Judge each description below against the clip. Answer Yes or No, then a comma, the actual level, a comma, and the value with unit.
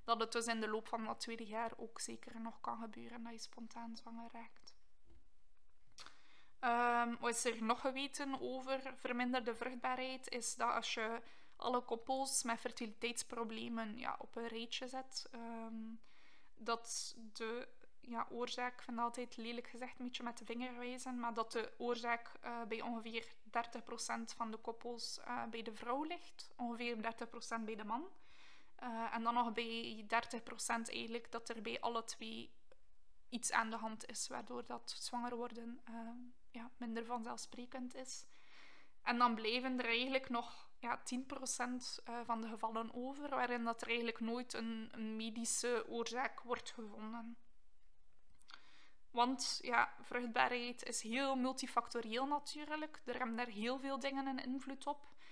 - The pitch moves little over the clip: Yes, narrow, 1.4 semitones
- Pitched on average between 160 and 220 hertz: No, high, 235 Hz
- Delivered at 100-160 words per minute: Yes, average, 155 wpm